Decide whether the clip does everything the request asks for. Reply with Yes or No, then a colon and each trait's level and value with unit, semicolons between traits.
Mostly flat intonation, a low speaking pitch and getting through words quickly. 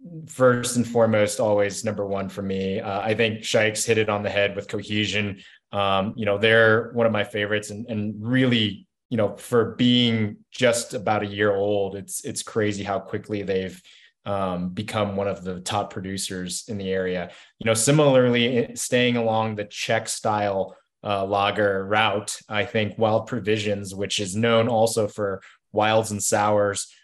No: narrow, 1.9 semitones; low, 105 Hz; average, 175 wpm